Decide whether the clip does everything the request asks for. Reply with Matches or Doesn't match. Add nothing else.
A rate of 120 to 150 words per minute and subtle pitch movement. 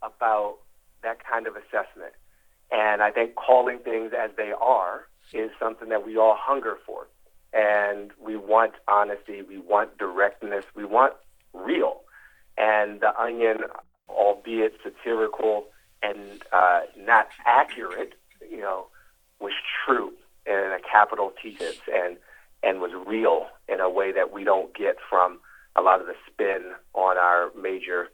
Matches